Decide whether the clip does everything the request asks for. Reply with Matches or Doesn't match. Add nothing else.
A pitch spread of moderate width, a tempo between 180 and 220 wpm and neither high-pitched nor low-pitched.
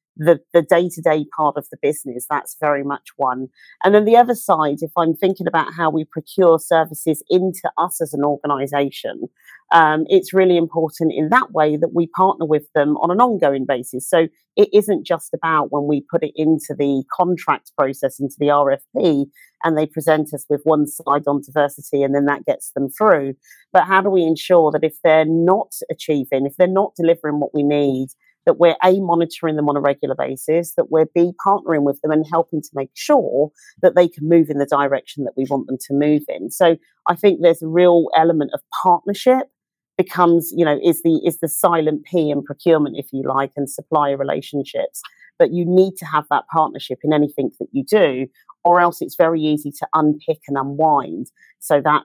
Matches